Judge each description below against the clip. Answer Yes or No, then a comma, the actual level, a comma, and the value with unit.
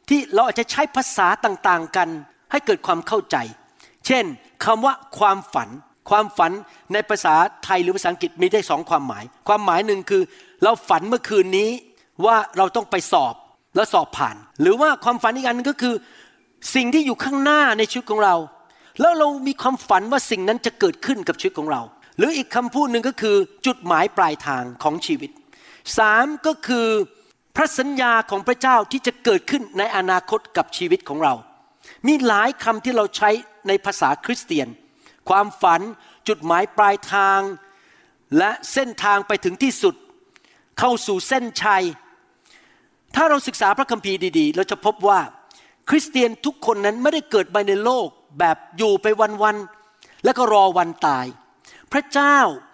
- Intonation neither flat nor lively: No, wide, 6.3 semitones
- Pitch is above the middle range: Yes, high, 235 Hz